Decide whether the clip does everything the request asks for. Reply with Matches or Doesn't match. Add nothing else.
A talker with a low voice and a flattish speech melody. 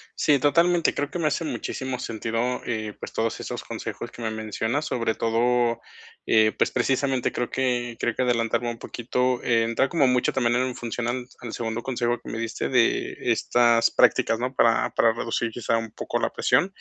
Matches